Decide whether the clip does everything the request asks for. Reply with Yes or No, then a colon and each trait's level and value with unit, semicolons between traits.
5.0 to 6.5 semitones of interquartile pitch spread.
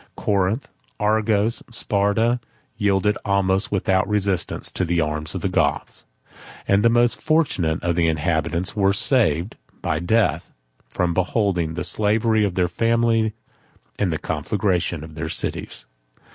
No: average, 4.3 semitones